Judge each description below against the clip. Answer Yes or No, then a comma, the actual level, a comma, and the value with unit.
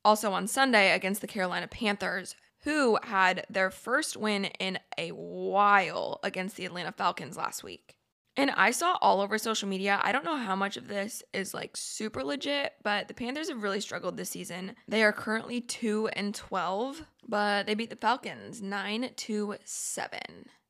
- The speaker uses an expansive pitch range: No, average, 3.1 semitones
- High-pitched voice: Yes, high, 210 Hz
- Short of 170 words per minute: No, average, 175 wpm